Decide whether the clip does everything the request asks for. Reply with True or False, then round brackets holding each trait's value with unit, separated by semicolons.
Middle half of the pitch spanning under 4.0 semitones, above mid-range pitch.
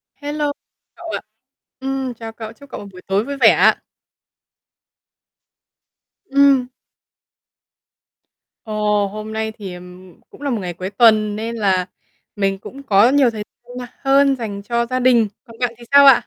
False (4.3 semitones; 230 Hz)